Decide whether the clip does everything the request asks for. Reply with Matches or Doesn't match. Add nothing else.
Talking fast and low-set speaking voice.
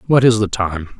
Matches